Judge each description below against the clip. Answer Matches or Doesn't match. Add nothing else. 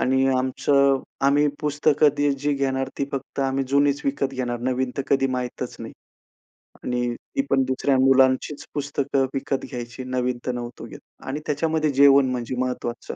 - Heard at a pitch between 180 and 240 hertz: Doesn't match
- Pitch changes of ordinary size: Doesn't match